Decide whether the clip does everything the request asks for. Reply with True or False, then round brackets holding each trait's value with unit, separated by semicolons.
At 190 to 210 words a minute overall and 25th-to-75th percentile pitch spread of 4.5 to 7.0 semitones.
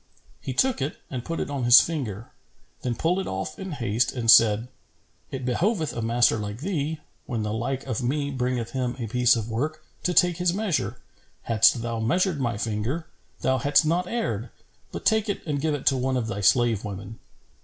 True (200 wpm; 5.3 semitones)